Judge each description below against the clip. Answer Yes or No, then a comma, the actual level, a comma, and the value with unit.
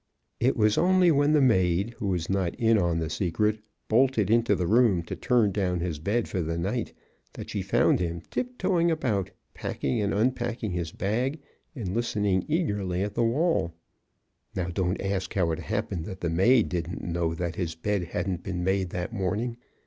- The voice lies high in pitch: No, low, 100 Hz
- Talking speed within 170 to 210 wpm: Yes, average, 185 wpm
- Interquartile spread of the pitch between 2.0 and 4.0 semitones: No, average, 5.0 semitones